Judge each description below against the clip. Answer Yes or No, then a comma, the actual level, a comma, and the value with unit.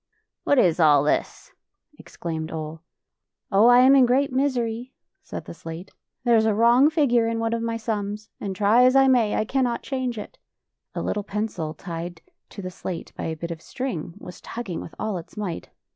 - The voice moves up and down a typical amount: No, wide, 5.9 semitones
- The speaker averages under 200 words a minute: No, fast, 205 wpm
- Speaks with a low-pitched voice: No, high, 220 Hz